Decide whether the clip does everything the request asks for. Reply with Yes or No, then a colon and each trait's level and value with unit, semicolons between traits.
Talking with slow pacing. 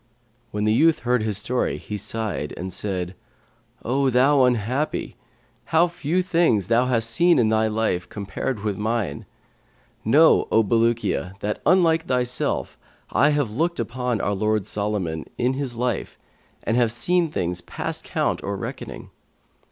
No: average, 150 wpm